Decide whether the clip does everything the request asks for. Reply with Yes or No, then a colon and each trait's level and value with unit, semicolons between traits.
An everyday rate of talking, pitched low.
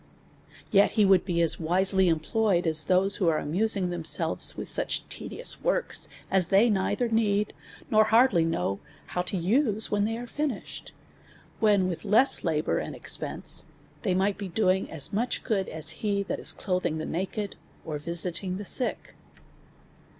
No: average, 165 wpm; high, 195 Hz